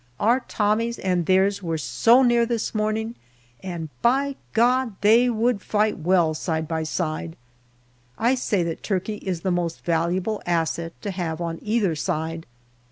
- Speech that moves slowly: No, average, 155 wpm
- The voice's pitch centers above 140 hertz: Yes, high, 190 Hz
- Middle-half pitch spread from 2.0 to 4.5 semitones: No, average, 5.2 semitones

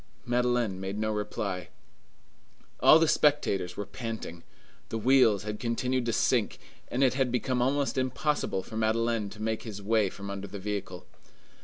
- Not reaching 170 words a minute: Yes, average, 160 wpm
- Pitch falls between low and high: No, low, 110 Hz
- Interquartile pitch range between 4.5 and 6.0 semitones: No, average, 3.7 semitones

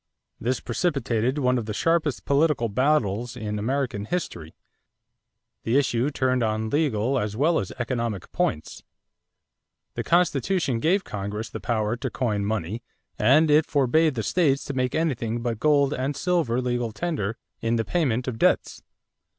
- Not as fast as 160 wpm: Yes, average, 150 wpm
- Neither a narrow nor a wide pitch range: Yes, average, 4.8 semitones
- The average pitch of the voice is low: Yes, low, 125 Hz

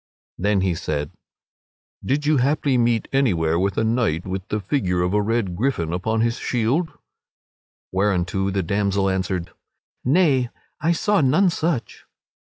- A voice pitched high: No, low, 105 Hz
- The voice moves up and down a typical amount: No, wide, 6.2 semitones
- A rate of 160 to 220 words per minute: No, average, 145 wpm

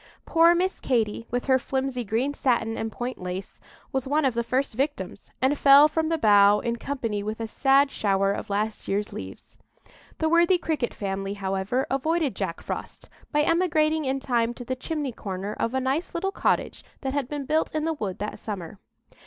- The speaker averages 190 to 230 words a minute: Yes, average, 195 wpm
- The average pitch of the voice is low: No, very high, 255 Hz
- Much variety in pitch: Yes, wide, 5.9 semitones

